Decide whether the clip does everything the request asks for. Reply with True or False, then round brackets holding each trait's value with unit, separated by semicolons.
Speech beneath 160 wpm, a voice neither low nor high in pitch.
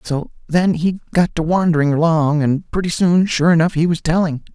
False (200 wpm; 165 Hz)